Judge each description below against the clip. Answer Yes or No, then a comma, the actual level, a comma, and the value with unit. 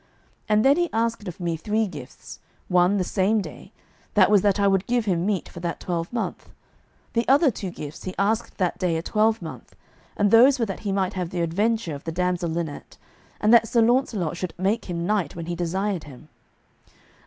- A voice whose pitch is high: Yes, high, 195 Hz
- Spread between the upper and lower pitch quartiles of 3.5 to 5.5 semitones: Yes, average, 4.2 semitones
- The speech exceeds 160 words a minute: Yes, average, 200 wpm